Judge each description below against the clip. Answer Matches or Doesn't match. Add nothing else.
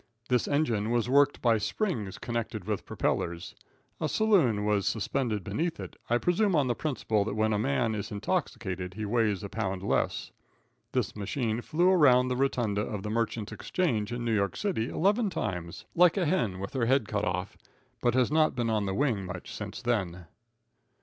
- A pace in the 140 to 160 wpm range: Doesn't match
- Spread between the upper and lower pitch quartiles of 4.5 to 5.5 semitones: Matches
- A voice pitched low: Matches